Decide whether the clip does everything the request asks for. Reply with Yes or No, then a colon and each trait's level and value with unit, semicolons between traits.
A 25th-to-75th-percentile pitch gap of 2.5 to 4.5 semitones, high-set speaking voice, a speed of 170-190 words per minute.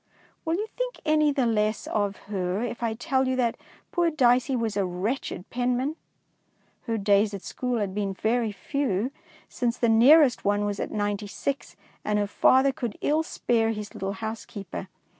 Yes: average, 4.1 semitones; high, 225 Hz; average, 175 wpm